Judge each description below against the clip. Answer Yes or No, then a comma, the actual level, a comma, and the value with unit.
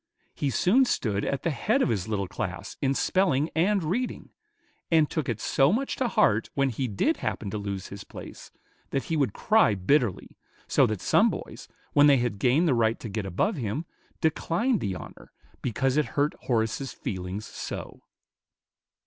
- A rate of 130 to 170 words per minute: No, average, 180 wpm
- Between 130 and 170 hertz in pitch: Yes, low, 135 Hz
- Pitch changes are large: Yes, wide, 7.4 semitones